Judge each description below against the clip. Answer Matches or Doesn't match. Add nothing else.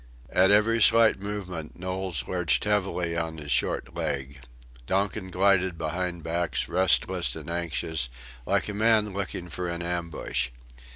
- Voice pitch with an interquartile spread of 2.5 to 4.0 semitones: Matches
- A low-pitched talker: Matches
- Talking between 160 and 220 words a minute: Doesn't match